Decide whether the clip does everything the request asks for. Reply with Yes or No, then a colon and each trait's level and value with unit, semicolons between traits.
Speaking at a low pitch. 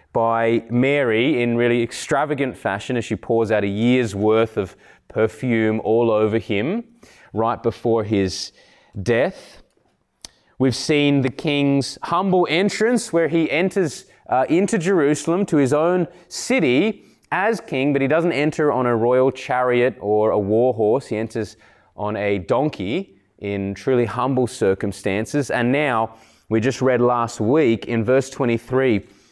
Yes: low, 125 Hz